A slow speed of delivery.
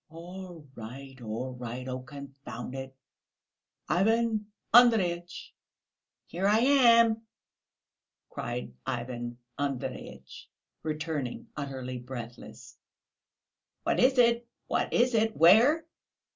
Yes: slow, 90 wpm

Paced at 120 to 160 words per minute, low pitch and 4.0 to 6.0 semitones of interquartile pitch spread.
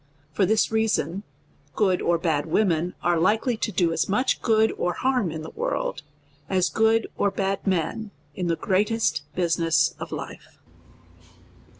No: average, 155 wpm; high, 190 Hz; average, 4.6 semitones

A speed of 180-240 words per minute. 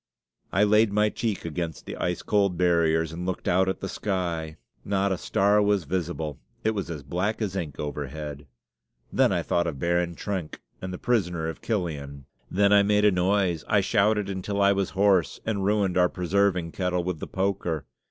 Yes: average, 190 wpm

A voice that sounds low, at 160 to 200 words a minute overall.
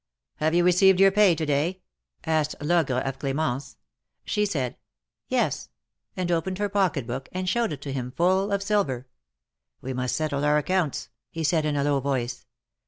No: medium, 155 Hz; average, 175 wpm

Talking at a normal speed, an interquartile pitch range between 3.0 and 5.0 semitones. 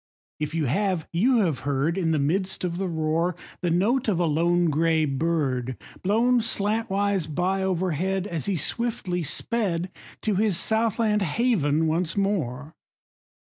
Yes: average, 150 wpm; average, 4.3 semitones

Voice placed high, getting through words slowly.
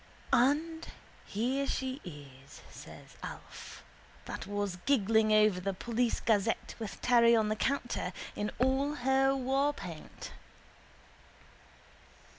Yes: high, 235 Hz; slow, 105 wpm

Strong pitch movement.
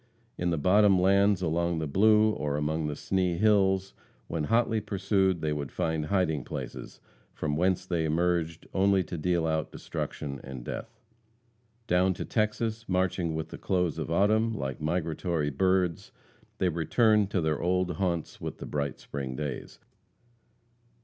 No: average, 3.6 semitones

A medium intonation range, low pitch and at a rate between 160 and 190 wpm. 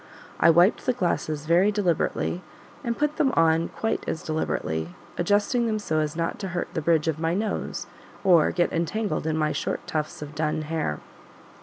No: average, 4.6 semitones; medium, 165 Hz; average, 180 wpm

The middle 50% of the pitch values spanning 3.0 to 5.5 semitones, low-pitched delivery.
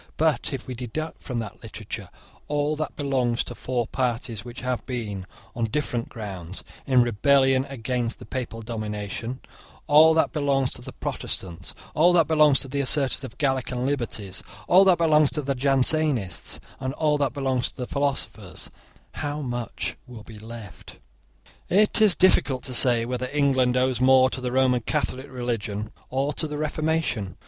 Yes: average, 3.5 semitones; low, 130 Hz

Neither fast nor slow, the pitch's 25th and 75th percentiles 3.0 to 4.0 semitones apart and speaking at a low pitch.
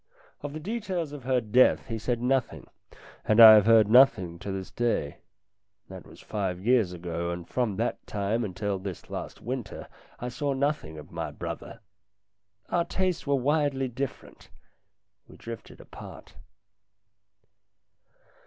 No: average, 145 wpm; wide, 5.6 semitones; low, 115 Hz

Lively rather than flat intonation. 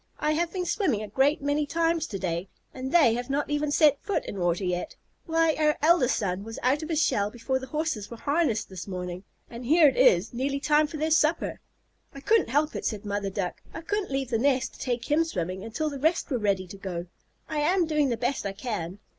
Yes: wide, 7.0 semitones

